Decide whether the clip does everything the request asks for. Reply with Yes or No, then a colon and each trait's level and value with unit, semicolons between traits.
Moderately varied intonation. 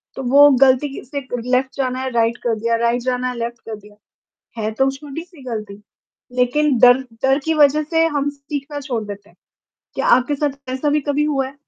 Yes: average, 3.0 semitones